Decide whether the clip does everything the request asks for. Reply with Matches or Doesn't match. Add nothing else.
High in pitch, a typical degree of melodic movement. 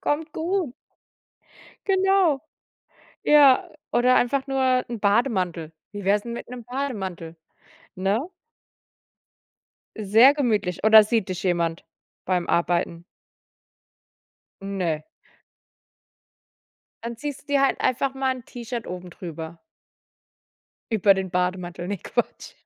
Doesn't match